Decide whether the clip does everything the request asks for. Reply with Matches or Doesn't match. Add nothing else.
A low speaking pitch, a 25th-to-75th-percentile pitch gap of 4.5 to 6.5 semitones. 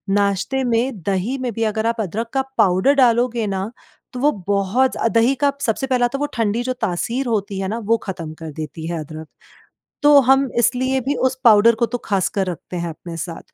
Doesn't match